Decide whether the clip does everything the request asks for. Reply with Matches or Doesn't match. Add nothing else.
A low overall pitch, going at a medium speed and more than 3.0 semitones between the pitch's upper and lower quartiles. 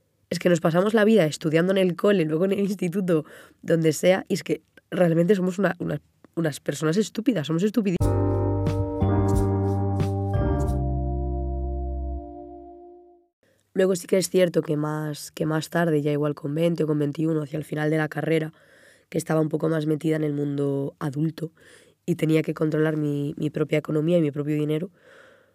Doesn't match